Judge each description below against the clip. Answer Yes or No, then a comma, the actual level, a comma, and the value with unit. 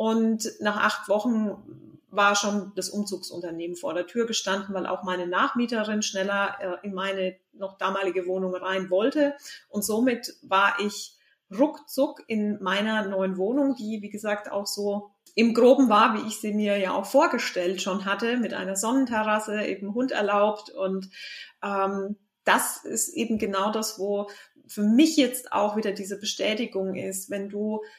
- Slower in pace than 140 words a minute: No, average, 160 wpm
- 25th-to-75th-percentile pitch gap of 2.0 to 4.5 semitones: Yes, narrow, 2.4 semitones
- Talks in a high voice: Yes, high, 205 Hz